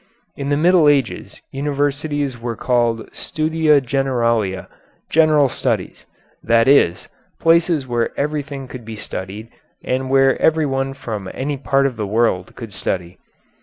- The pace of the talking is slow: Yes, slow, 130 wpm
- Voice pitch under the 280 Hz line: Yes, low, 135 Hz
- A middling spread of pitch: Yes, average, 3.9 semitones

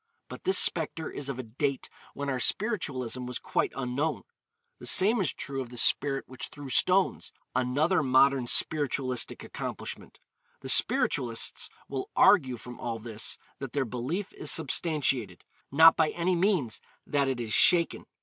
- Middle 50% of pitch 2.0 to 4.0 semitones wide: No, average, 4.4 semitones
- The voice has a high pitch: No, low, 135 Hz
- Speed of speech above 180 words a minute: No, average, 155 wpm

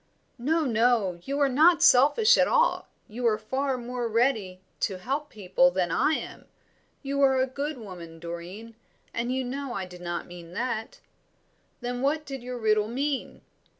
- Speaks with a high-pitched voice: Yes, high, 245 Hz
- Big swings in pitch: Yes, wide, 5.7 semitones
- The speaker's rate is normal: Yes, average, 170 wpm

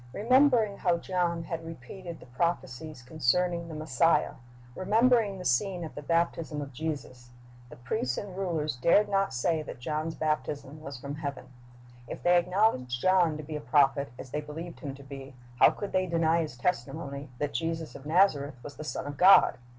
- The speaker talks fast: No, average, 185 wpm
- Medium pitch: Yes, medium, 160 Hz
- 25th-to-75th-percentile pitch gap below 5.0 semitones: Yes, average, 4.1 semitones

